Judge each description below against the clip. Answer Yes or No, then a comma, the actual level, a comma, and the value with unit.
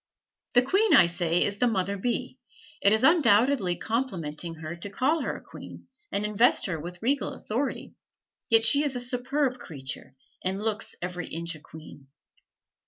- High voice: Yes, high, 210 Hz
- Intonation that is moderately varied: No, wide, 6.4 semitones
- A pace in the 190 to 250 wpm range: No, average, 170 wpm